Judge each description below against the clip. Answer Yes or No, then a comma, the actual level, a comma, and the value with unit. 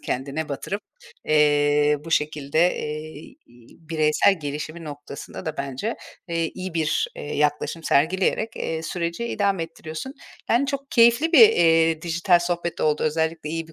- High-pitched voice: No, medium, 160 Hz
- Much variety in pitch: No, average, 2.9 semitones